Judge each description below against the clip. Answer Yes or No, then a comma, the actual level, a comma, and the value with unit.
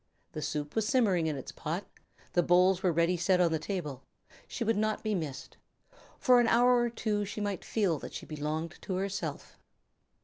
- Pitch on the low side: No, medium, 185 Hz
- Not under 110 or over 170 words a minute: No, average, 195 wpm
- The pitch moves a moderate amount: Yes, average, 4.9 semitones